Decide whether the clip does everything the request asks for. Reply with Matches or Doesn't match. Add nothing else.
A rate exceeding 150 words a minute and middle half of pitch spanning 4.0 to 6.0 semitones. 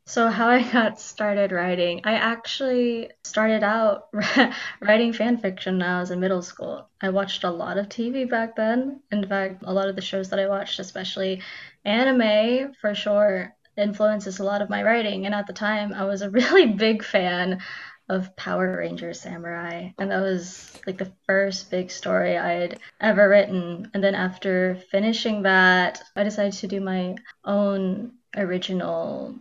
Doesn't match